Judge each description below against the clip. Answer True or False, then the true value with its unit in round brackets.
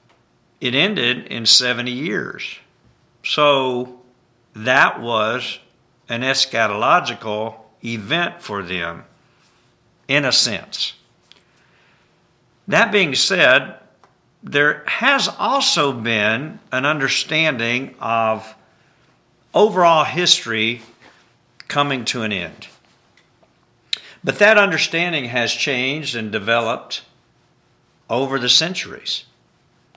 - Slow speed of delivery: True (85 wpm)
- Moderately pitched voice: False (125 Hz)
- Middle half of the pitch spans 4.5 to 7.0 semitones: True (4.8 semitones)